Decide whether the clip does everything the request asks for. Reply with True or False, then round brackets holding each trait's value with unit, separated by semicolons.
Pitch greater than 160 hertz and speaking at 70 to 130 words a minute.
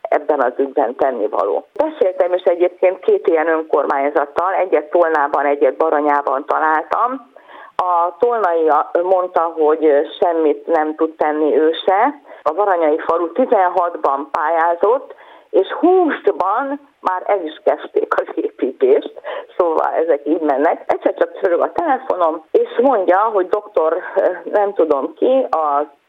True (185 Hz; 125 wpm)